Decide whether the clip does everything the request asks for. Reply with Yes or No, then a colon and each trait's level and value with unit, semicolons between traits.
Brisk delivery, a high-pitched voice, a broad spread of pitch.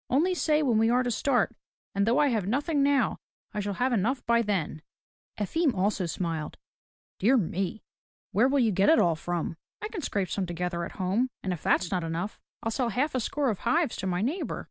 Yes: fast, 220 wpm; high, 220 Hz; wide, 6.2 semitones